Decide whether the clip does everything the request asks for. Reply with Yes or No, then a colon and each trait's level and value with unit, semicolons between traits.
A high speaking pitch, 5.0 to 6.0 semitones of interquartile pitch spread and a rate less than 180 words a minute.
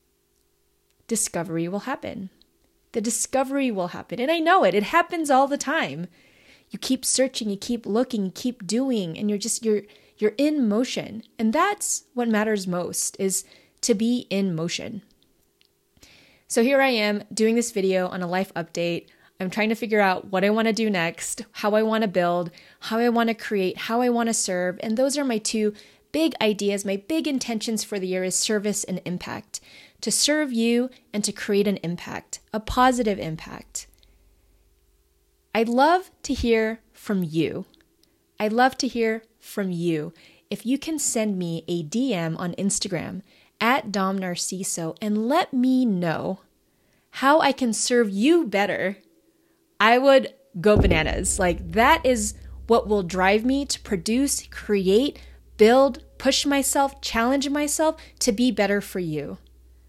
Yes: high, 220 Hz; average, 5.3 semitones; average, 165 wpm